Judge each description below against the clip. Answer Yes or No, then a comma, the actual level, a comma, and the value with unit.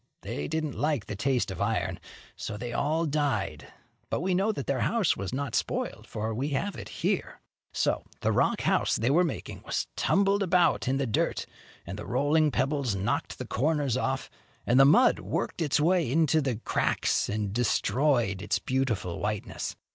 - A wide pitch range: Yes, wide, 5.7 semitones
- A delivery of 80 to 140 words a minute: No, average, 180 wpm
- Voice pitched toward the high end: No, low, 135 Hz